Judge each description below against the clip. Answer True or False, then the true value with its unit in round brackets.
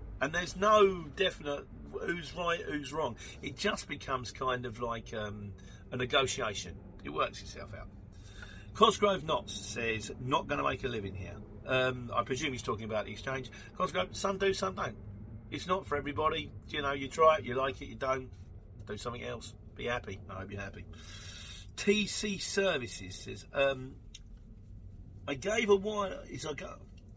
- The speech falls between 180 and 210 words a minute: False (170 wpm)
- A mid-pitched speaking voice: False (115 Hz)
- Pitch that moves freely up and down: True (6.3 semitones)